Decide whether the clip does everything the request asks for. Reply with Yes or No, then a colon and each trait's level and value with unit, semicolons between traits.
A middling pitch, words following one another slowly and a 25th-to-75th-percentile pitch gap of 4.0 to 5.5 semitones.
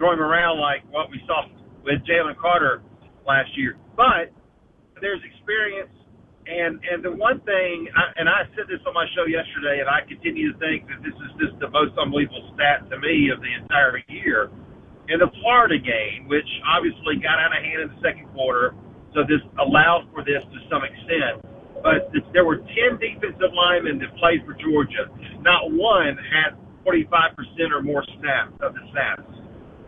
No: medium, 170 Hz; average, 185 wpm; average, 5.0 semitones